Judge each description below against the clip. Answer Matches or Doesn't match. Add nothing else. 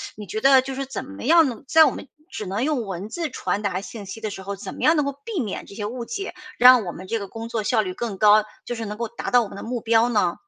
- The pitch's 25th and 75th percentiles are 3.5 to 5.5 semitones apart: Matches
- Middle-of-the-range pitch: Doesn't match